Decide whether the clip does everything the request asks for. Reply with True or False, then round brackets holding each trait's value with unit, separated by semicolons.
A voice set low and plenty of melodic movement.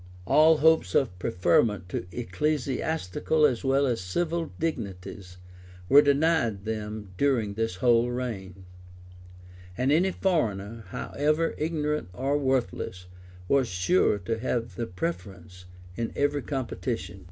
True (120 Hz; 7.2 semitones)